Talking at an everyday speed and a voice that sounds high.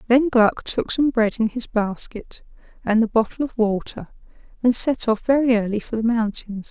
Yes: average, 190 wpm; high, 230 Hz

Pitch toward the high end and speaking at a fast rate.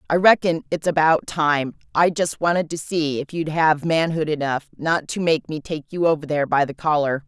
No: medium, 155 Hz; fast, 215 wpm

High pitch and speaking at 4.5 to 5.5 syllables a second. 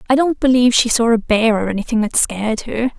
No: high, 230 Hz; 6.2 syllables/s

